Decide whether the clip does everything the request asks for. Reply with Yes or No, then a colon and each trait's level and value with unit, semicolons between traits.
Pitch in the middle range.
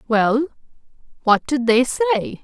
No: high, 245 Hz